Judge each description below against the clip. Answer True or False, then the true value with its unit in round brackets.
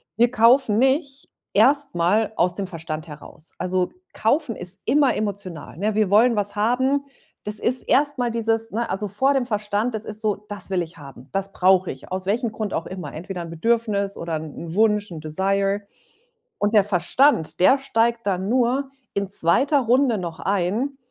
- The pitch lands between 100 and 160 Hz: False (210 Hz)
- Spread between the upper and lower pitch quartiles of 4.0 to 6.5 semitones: True (4.5 semitones)